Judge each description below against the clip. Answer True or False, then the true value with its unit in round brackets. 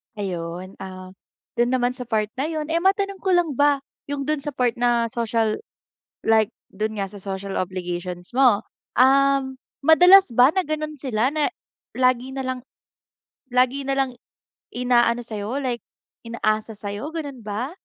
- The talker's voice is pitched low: False (250 Hz)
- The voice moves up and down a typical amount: True (4.7 semitones)